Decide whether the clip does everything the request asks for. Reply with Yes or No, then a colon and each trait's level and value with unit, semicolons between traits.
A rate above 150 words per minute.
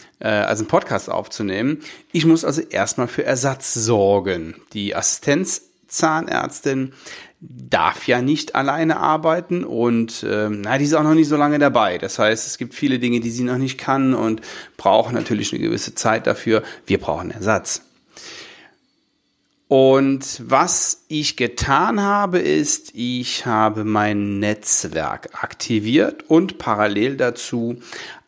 No: average, 135 wpm